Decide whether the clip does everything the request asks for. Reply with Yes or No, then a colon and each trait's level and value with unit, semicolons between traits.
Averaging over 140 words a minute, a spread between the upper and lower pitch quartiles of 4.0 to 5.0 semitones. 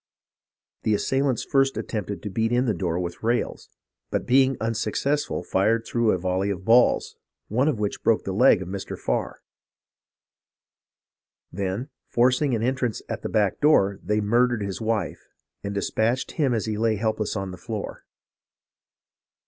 No: average, 160 wpm; average, 3.6 semitones